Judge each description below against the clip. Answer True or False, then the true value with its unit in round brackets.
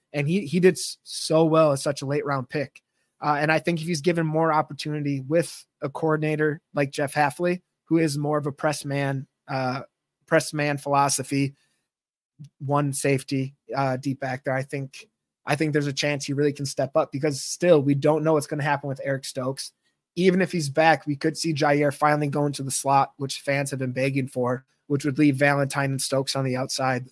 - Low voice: False (145 Hz)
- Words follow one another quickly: True (210 wpm)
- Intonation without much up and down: True (2.1 semitones)